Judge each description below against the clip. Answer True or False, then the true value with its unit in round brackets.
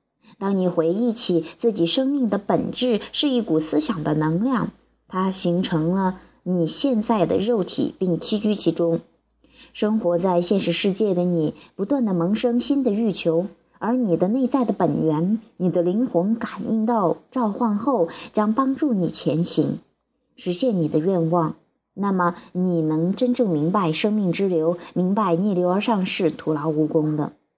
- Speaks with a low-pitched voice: False (190 Hz)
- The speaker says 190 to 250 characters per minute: True (235 characters per minute)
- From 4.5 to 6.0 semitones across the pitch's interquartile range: True (5.2 semitones)